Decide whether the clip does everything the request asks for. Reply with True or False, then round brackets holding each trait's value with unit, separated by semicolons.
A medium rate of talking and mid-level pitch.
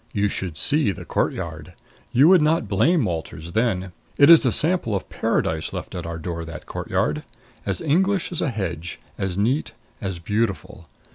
False (170 wpm; 105 Hz)